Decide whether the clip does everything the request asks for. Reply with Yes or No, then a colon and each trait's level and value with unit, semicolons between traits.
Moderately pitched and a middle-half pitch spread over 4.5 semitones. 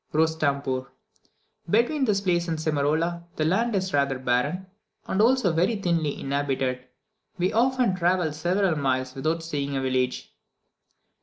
Yes: medium, 160 Hz; average, 5.1 semitones